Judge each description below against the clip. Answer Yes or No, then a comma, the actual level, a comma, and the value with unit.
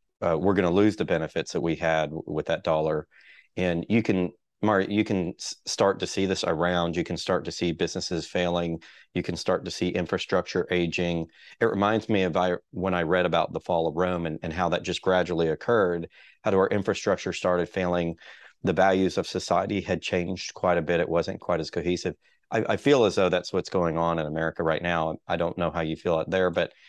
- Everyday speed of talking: No, fast, 220 wpm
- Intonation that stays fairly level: Yes, narrow, 1.9 semitones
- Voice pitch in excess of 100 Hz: No, very low, 90 Hz